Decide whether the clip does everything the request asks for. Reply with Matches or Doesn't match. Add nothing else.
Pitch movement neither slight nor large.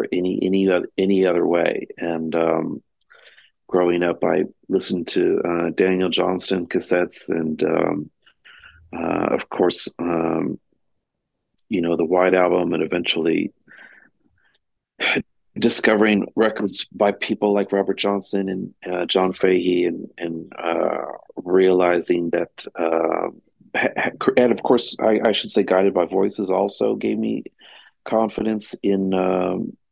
Doesn't match